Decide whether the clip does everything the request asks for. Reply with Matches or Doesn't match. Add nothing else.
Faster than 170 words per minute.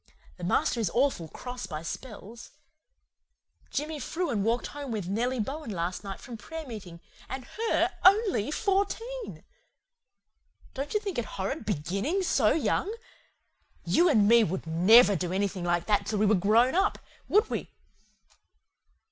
Doesn't match